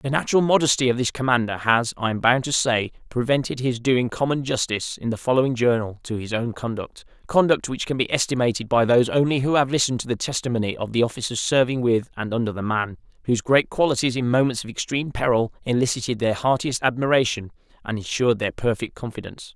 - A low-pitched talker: Yes, low, 125 Hz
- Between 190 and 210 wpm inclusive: Yes, average, 195 wpm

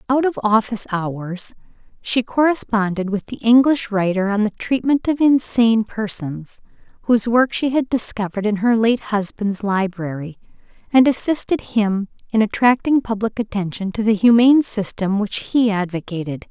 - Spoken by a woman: Yes, female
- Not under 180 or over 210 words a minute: No, average, 145 wpm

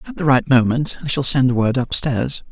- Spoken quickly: Yes, fast, 215 wpm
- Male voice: Yes, male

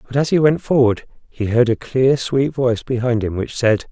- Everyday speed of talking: No, fast, 230 wpm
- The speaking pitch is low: Yes, low, 125 Hz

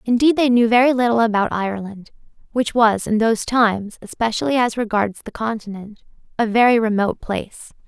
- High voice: Yes, high, 225 Hz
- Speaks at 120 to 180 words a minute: Yes, average, 160 wpm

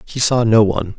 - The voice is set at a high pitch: No, low, 105 Hz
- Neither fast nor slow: No, fast, 245 wpm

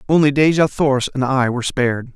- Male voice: Yes, male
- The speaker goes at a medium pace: Yes, average, 195 wpm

